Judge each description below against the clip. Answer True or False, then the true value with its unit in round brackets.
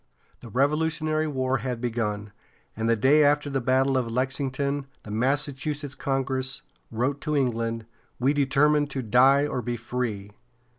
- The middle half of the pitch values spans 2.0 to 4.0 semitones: True (3.1 semitones)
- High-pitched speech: False (135 Hz)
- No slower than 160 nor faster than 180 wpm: False (145 wpm)